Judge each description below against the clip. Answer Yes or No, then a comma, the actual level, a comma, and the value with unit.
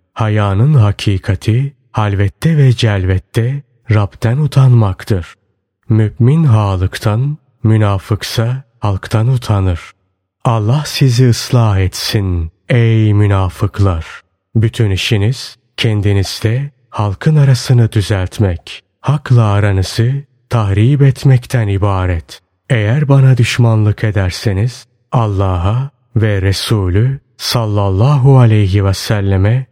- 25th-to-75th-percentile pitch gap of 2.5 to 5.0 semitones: Yes, average, 4.0 semitones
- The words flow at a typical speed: No, slow, 80 wpm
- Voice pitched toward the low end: Yes, low, 110 Hz